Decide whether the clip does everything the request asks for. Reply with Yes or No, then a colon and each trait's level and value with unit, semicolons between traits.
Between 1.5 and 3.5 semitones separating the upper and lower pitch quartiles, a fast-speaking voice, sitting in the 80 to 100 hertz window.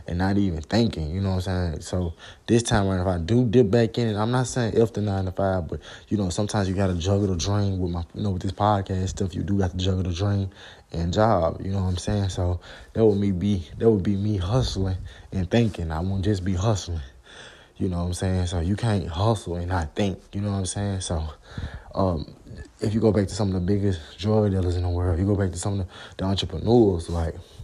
Yes: narrow, 2.6 semitones; fast, 265 wpm; very low, 95 Hz